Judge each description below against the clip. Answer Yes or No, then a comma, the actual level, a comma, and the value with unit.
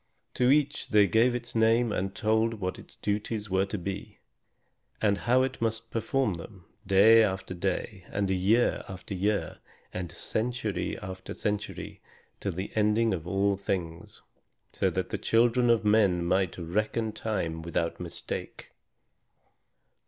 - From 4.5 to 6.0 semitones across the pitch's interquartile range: No, average, 3.2 semitones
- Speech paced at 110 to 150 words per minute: Yes, average, 145 wpm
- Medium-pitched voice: No, low, 105 Hz